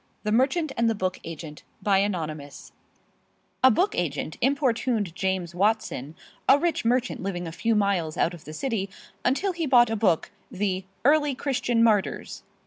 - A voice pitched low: No, high, 210 Hz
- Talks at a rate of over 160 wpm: No, average, 155 wpm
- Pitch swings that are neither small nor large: No, wide, 6.2 semitones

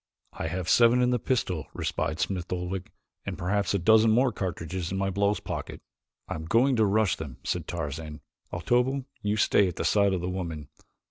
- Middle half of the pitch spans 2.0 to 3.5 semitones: No, average, 4.3 semitones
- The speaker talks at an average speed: Yes, average, 190 wpm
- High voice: No, very low, 95 Hz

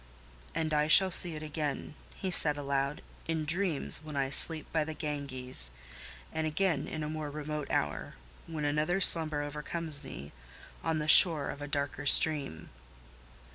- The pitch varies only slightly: Yes, narrow, 2.0 semitones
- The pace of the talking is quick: No, average, 150 wpm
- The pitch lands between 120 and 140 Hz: No, medium, 150 Hz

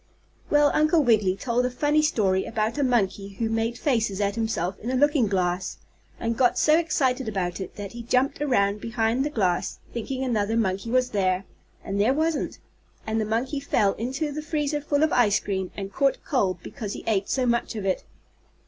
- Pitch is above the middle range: Yes, high, 230 Hz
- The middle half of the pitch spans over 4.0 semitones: Yes, average, 5.1 semitones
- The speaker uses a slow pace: No, average, 195 wpm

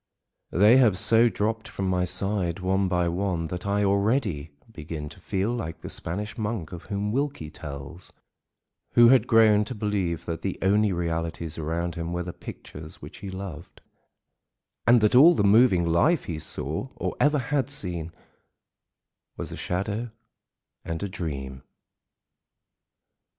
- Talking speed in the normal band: Yes, average, 150 wpm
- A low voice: Yes, very low, 95 Hz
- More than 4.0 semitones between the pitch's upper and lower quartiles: Yes, average, 4.4 semitones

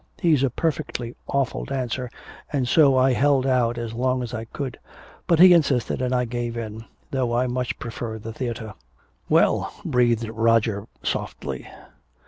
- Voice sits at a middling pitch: No, low, 125 Hz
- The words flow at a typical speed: Yes, average, 155 wpm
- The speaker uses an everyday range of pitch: No, narrow, 2.3 semitones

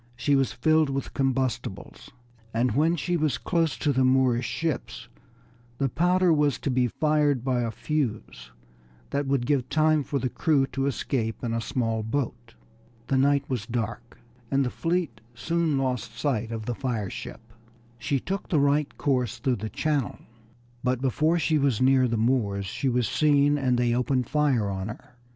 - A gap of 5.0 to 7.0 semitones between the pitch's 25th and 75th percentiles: No, average, 3.6 semitones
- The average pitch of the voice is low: Yes, low, 130 Hz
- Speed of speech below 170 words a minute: No, average, 175 wpm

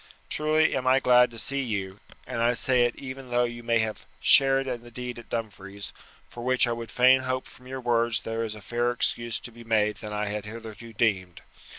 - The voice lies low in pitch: Yes, low, 120 Hz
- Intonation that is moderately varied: No, narrow, 2.3 semitones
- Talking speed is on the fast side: Yes, fast, 220 wpm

